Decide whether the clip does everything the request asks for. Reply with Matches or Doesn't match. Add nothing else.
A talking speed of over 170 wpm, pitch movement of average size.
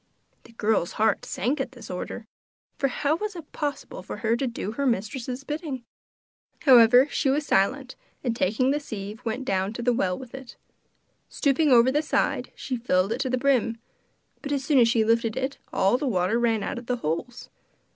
Matches